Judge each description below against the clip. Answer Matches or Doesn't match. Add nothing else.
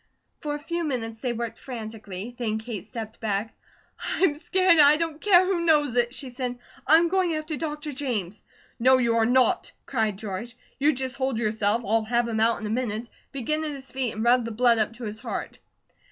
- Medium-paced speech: Doesn't match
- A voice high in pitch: Matches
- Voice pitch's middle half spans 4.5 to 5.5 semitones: Matches